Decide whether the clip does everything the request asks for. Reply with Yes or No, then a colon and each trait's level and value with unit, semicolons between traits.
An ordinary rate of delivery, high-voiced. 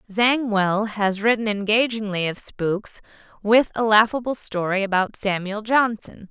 No: slow, 125 wpm; high, 210 Hz